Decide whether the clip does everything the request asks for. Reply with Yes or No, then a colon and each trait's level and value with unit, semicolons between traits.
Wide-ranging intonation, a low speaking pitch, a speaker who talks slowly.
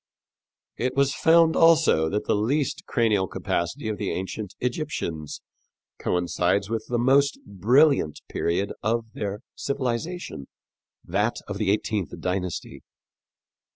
Yes: wide, 6.5 semitones; low, 110 Hz; slow, 120 wpm